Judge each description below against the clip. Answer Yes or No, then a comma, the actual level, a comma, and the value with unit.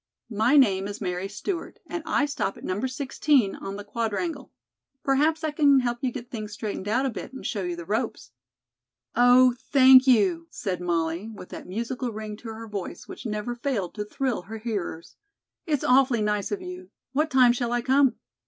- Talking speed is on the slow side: No, average, 190 wpm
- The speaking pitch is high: Yes, high, 235 Hz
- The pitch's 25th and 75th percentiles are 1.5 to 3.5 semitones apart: No, average, 4.5 semitones